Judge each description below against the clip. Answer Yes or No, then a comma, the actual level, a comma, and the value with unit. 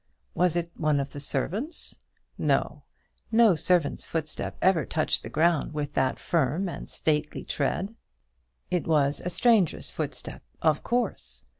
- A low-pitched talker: No, medium, 160 Hz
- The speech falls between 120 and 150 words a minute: Yes, average, 140 wpm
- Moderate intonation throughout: Yes, average, 3.5 semitones